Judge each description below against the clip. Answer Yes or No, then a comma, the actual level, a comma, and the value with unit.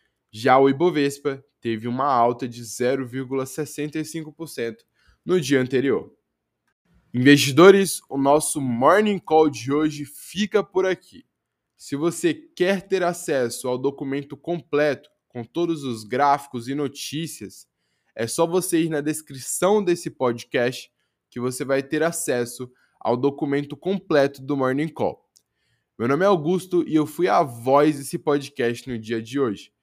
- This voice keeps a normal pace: Yes, average, 140 wpm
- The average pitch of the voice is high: No, medium, 145 Hz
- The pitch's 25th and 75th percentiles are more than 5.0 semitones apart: No, average, 4.3 semitones